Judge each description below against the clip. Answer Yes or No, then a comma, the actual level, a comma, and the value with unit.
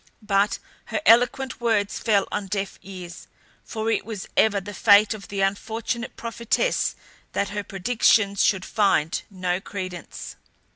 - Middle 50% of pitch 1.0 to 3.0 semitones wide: Yes, narrow, 2.5 semitones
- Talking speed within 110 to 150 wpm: Yes, average, 140 wpm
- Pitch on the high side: Yes, high, 205 Hz